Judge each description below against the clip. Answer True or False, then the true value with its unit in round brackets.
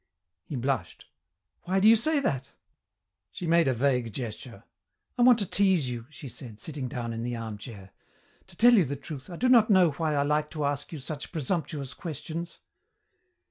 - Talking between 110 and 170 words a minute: False (185 wpm)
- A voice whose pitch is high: False (145 Hz)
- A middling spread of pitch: False (5.8 semitones)